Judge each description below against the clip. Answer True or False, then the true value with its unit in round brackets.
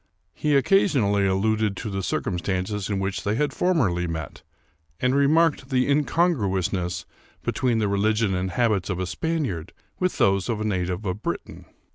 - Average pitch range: False (6.0 semitones)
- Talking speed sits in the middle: True (160 wpm)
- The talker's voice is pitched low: True (105 Hz)